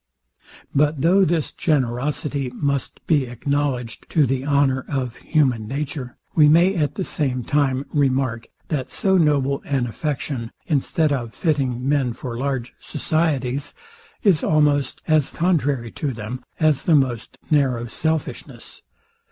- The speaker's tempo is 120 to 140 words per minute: Yes, slow, 135 wpm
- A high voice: No, medium, 140 Hz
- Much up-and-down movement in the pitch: No, average, 3.0 semitones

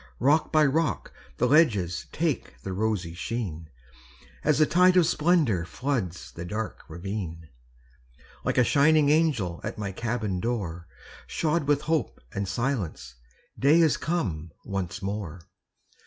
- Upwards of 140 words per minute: No, slow, 135 wpm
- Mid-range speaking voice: No, low, 110 Hz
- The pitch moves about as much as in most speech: No, wide, 9.0 semitones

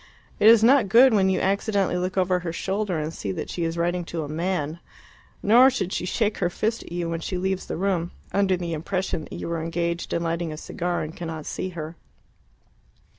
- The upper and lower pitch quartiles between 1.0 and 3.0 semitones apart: Yes, average, 2.7 semitones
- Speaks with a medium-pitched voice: Yes, medium, 180 Hz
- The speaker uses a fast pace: Yes, fast, 220 wpm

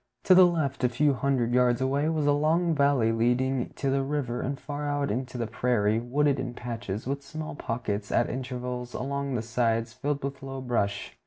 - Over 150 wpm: Yes, average, 195 wpm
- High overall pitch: No, low, 130 Hz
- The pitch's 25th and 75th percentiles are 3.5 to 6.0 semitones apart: No, average, 2.9 semitones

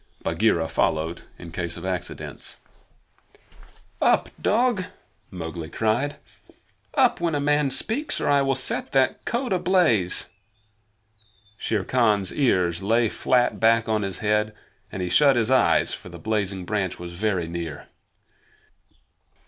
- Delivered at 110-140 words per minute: Yes, slow, 135 wpm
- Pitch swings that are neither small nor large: No, wide, 7.3 semitones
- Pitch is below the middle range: Yes, low, 110 Hz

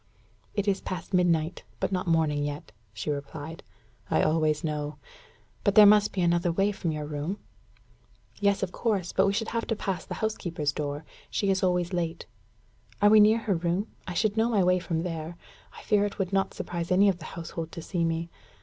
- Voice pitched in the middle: Yes, medium, 175 Hz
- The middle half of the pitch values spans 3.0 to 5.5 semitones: Yes, average, 3.7 semitones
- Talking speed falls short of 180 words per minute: No, fast, 205 wpm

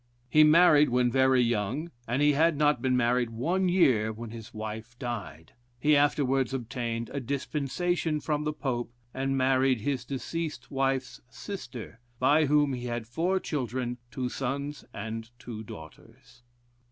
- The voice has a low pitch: Yes, low, 130 Hz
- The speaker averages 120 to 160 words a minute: Yes, average, 150 wpm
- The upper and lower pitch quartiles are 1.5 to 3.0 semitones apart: No, average, 3.8 semitones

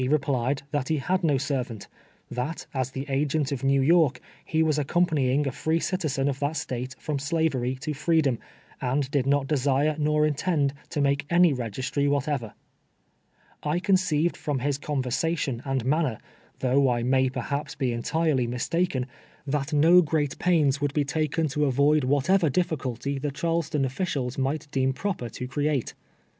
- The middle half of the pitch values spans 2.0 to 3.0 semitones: Yes, average, 2.7 semitones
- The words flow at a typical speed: Yes, average, 165 wpm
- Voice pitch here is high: No, medium, 140 Hz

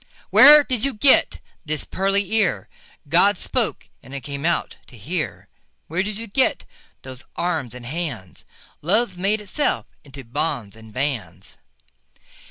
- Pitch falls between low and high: Yes, medium, 165 Hz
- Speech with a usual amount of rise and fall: No, wide, 8.0 semitones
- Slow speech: Yes, slow, 130 wpm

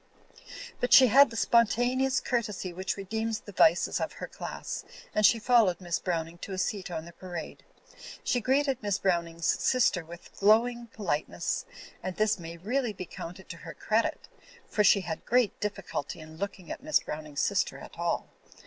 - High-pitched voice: Yes, high, 200 Hz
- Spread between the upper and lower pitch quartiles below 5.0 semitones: No, average, 5.3 semitones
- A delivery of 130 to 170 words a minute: No, average, 180 wpm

